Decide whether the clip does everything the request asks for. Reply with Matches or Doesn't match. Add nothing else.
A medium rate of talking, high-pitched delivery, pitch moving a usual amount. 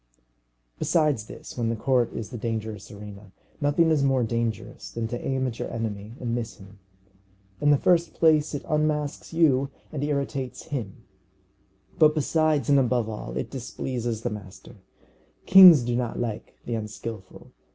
Doesn't match